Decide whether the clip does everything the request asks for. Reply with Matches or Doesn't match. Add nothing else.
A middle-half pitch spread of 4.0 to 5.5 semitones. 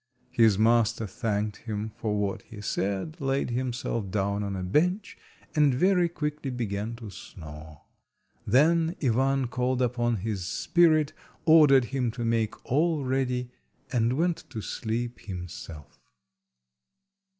Matches